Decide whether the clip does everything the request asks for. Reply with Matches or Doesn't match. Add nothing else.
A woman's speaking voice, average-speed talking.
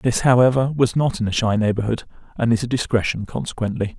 Doesn't match